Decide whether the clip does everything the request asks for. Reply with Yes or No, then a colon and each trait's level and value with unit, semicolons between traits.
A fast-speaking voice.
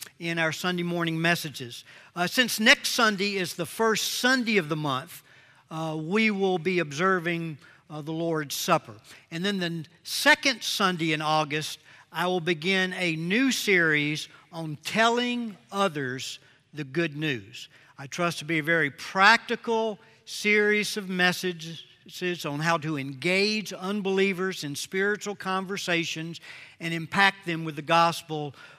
No: average, 140 wpm